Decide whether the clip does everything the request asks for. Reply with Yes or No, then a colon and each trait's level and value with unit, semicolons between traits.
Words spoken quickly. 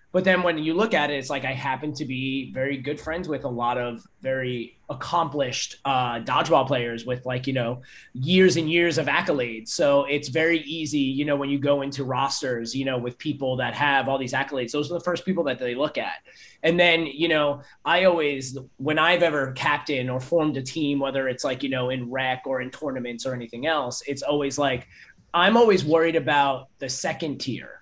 Yes: fast, 215 wpm